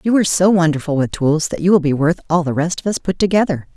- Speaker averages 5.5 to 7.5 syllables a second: Yes, 6.3 syllables/s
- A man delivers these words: No, female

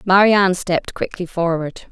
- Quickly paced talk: No, average, 155 wpm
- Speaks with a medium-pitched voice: Yes, medium, 180 Hz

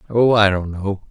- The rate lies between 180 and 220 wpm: Yes, fast, 215 wpm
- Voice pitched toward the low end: Yes, low, 100 Hz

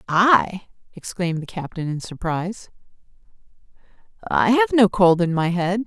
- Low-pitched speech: No, high, 190 Hz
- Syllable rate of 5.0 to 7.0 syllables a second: No, 4.7 syllables/s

